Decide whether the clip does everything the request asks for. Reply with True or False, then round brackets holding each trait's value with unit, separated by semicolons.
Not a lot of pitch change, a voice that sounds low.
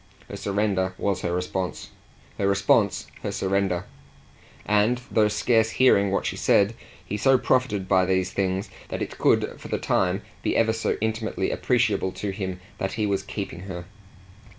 True (2.3 semitones; 100 Hz)